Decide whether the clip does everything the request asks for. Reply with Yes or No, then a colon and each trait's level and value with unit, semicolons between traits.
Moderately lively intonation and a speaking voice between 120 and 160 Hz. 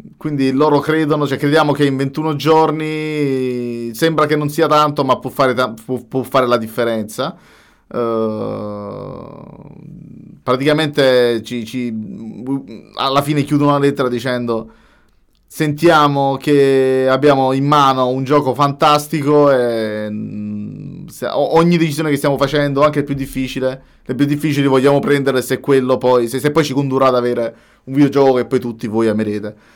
Yes: average, 3.0 semitones; low, 135 Hz